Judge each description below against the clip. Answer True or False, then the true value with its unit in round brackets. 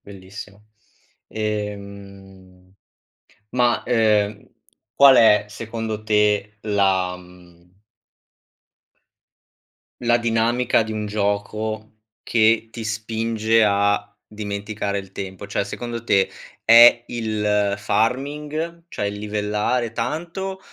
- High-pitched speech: False (105 Hz)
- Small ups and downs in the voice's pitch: True (2.2 semitones)